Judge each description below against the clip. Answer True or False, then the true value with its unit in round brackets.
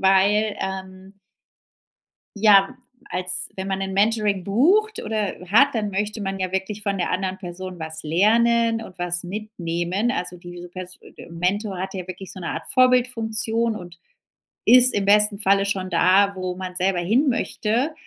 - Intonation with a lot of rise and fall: False (2.8 semitones)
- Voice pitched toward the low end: False (195 Hz)